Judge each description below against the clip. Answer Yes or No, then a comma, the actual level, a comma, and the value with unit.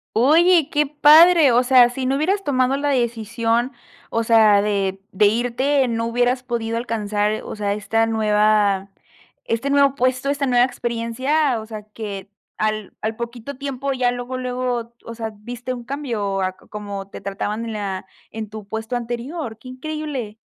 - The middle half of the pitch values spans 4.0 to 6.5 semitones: No, average, 3.4 semitones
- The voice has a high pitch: Yes, high, 235 Hz